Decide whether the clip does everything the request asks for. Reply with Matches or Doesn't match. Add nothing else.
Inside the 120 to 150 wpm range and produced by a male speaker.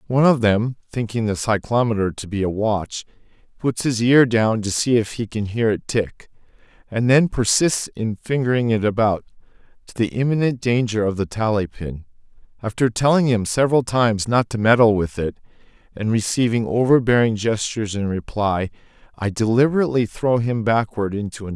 Doesn't match